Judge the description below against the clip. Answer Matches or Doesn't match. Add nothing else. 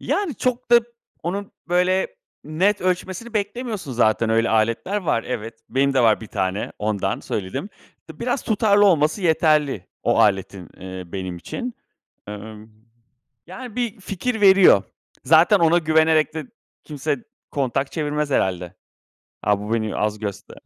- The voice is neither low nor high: Matches